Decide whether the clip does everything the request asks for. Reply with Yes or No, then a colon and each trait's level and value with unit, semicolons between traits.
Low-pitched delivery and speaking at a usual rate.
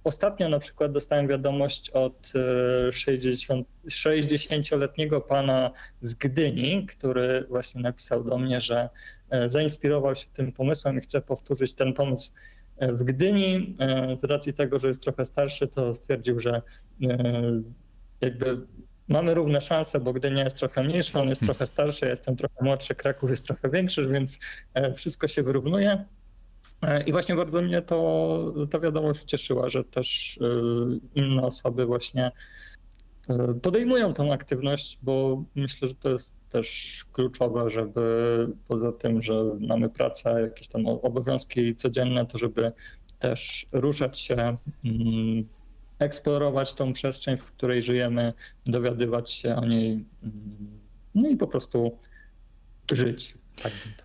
Yes: low, 130 Hz; average, 130 wpm